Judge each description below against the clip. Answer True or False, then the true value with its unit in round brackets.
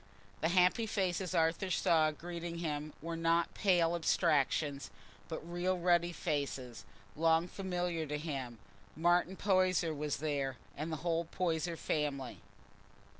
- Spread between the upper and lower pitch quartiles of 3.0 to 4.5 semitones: False (2.6 semitones)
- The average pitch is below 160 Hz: False (165 Hz)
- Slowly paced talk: True (120 wpm)